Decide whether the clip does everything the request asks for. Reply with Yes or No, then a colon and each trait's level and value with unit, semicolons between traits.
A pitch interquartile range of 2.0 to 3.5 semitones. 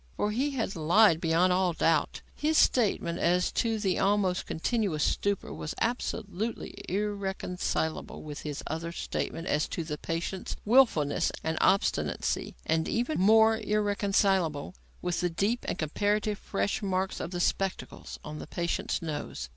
No: average, 4.3 semitones